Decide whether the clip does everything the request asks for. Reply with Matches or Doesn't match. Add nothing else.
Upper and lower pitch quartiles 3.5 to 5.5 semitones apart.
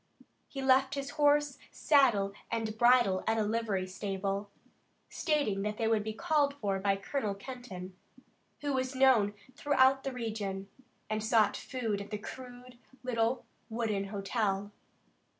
Matches